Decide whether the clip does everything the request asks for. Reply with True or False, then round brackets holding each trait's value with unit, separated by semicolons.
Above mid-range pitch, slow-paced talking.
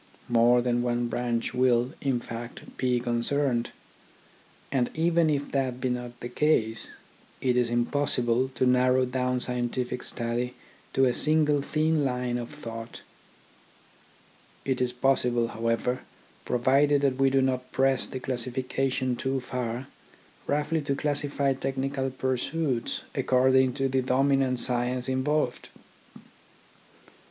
False (130 Hz; 125 wpm)